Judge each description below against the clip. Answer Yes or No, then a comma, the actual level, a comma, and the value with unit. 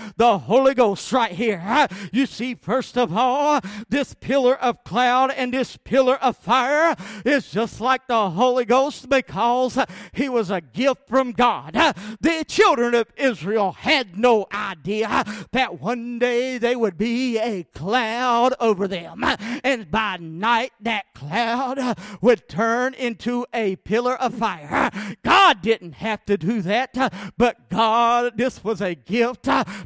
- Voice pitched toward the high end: Yes, high, 235 Hz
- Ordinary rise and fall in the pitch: Yes, average, 3.2 semitones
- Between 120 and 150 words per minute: Yes, average, 145 wpm